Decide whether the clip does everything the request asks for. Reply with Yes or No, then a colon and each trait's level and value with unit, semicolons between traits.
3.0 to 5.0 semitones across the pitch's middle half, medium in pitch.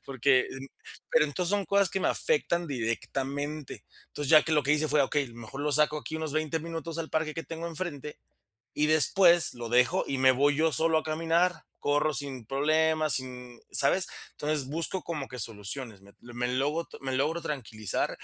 Yes: average, 3.5 semitones; medium, 150 Hz